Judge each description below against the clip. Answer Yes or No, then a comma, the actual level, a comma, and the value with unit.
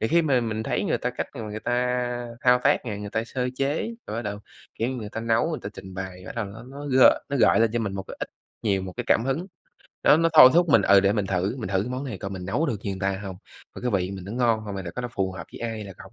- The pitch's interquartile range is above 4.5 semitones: No, average, 4.2 semitones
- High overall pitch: No, low, 110 Hz